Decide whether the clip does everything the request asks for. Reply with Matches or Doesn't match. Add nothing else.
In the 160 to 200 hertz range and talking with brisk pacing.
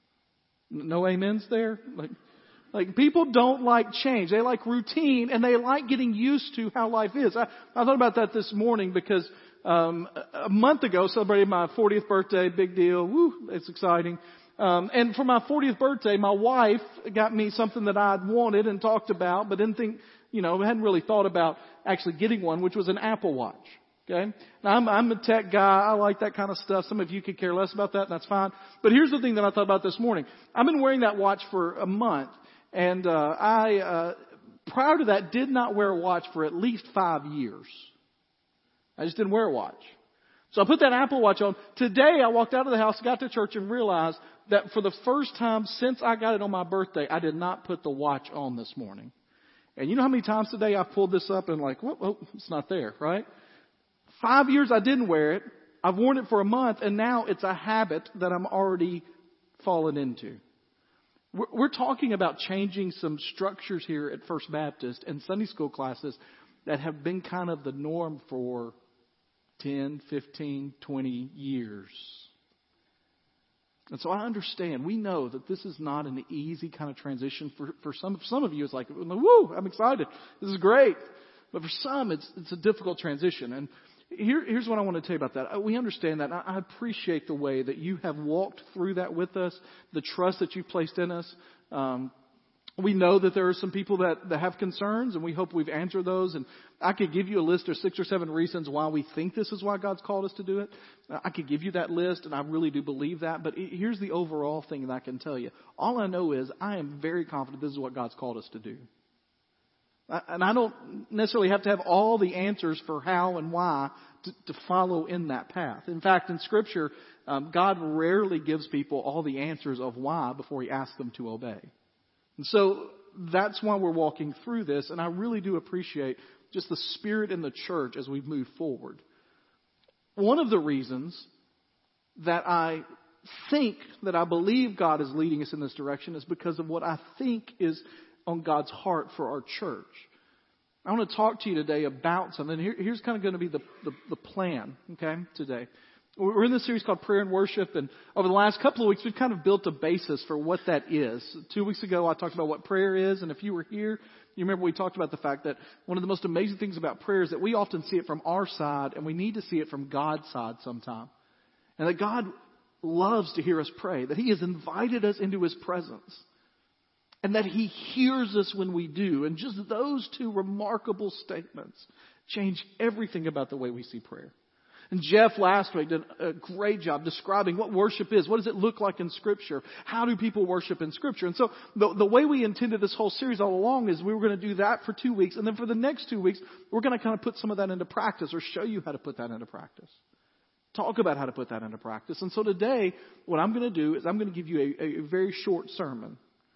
Matches